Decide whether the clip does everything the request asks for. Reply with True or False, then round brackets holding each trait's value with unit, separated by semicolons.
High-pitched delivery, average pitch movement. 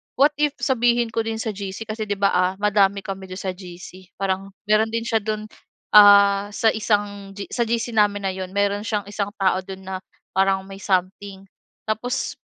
False (200 Hz; 2.3 semitones)